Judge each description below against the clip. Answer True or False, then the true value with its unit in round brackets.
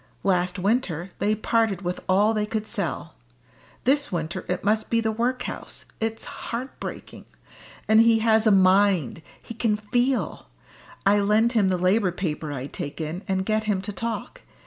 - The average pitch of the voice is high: True (210 Hz)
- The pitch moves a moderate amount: True (3.5 semitones)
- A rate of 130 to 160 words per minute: False (170 wpm)